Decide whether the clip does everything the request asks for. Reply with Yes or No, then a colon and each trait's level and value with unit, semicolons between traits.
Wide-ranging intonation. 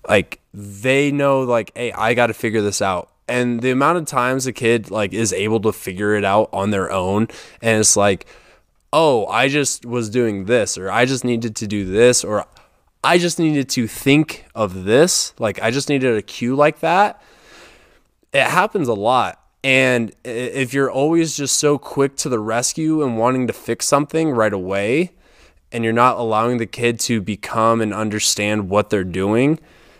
No: average, 3.9 semitones